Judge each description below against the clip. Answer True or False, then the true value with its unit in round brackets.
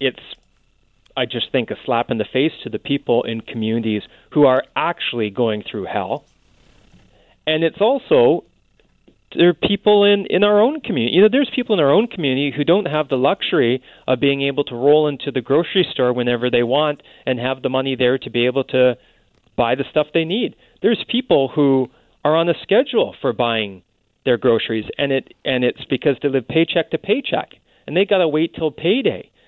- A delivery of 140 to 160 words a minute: False (200 wpm)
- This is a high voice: False (140 Hz)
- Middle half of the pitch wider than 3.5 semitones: True (5.2 semitones)